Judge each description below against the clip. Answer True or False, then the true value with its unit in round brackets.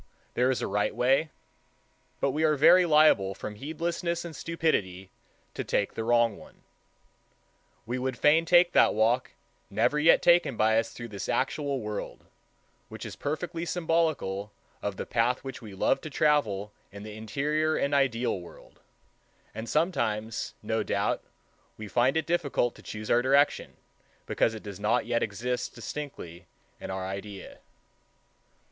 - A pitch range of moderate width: False (6.2 semitones)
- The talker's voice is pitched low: True (125 Hz)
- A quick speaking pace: False (155 wpm)